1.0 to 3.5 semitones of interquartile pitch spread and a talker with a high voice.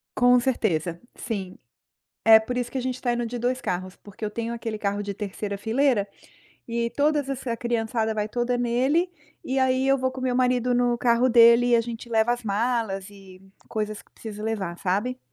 Yes: average, 2.9 semitones; high, 235 Hz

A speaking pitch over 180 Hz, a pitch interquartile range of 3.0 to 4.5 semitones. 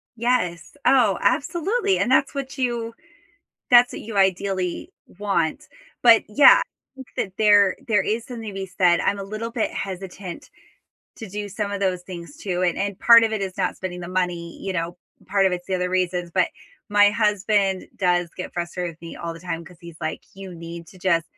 Yes: high, 190 Hz; average, 3.5 semitones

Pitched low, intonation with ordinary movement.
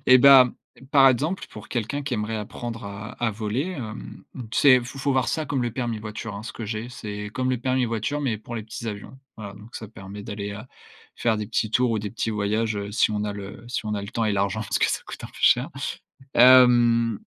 Yes: low, 115 Hz; average, 3.0 semitones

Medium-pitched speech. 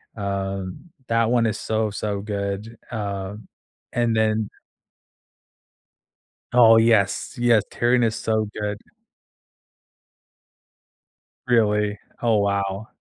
No: low, 110 Hz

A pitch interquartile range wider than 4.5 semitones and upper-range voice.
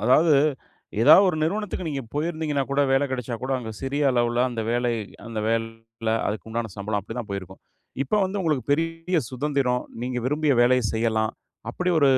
No: average, 5.0 semitones; low, 125 Hz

